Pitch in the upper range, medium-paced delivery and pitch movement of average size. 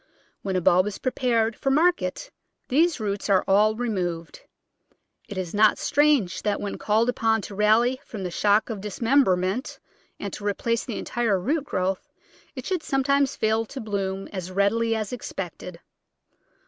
Yes: high, 215 Hz; average, 160 wpm; average, 4.3 semitones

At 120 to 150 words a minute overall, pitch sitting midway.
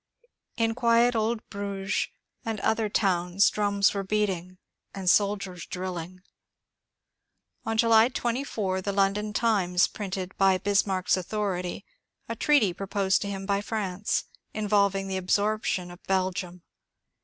No: slow, 135 wpm; high, 200 Hz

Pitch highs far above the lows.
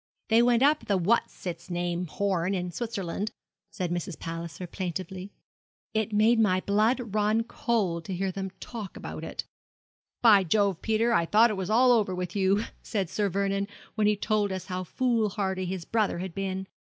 No: average, 3.1 semitones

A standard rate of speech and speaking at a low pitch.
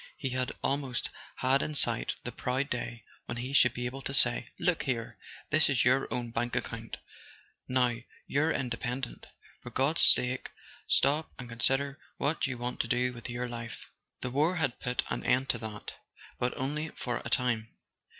Yes: average, 175 wpm; low, 125 Hz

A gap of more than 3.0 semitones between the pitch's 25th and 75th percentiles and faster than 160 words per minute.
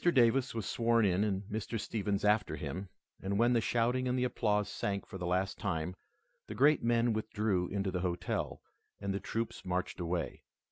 Yes: average, 3.4 semitones; average, 180 wpm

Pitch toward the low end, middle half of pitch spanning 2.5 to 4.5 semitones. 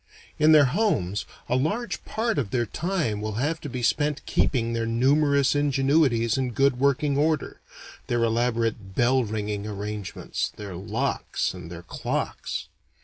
No: low, 125 Hz; average, 5.2 semitones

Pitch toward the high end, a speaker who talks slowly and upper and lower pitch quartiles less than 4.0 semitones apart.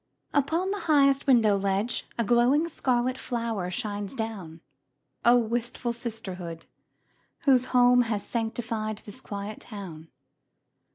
Yes: high, 230 Hz; slow, 115 wpm; average, 3.5 semitones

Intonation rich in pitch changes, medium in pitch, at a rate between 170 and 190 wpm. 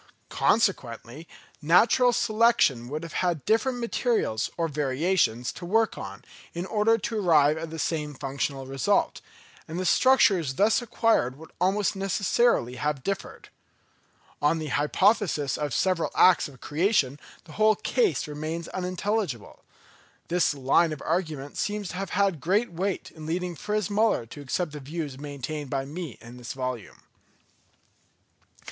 No: wide, 6.0 semitones; medium, 165 Hz; average, 145 wpm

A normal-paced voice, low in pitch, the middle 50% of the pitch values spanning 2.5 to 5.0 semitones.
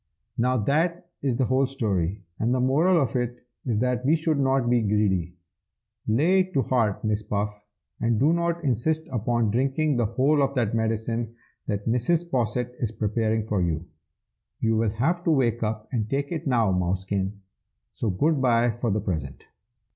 Yes: average, 175 wpm; low, 120 Hz; average, 4.3 semitones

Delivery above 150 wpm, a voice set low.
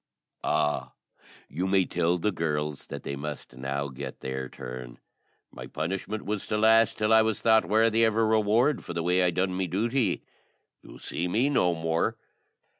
Yes: average, 180 wpm; very low, 90 Hz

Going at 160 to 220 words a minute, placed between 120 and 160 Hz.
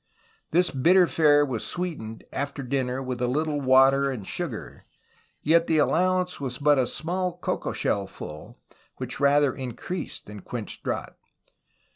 No: average, 150 wpm; medium, 140 Hz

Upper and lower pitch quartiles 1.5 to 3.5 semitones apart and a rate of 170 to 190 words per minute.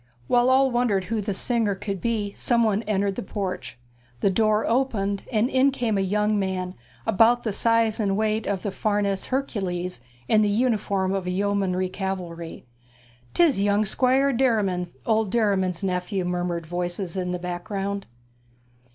No: average, 3.2 semitones; average, 160 wpm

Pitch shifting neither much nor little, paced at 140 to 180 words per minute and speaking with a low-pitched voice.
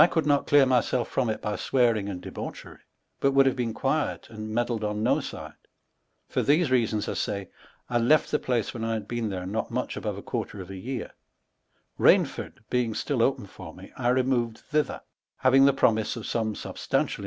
No: average, 3.5 semitones; average, 195 wpm; low, 120 Hz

